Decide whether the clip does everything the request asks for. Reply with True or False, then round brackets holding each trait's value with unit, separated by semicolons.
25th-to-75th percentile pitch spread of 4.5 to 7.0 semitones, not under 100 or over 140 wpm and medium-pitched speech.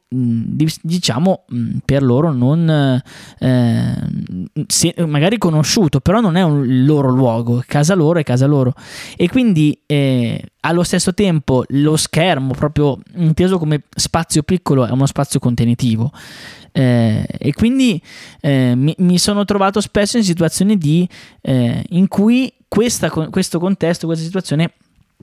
True (5.5 semitones; 130 wpm; 155 Hz)